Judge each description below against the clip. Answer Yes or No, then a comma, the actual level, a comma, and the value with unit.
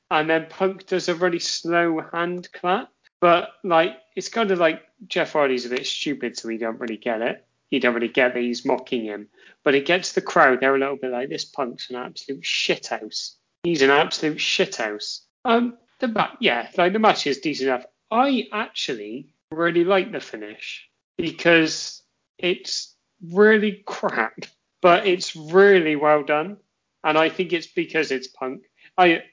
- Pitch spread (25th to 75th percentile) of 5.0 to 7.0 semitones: Yes, wide, 5.5 semitones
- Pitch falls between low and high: Yes, medium, 170 Hz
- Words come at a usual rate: Yes, average, 180 wpm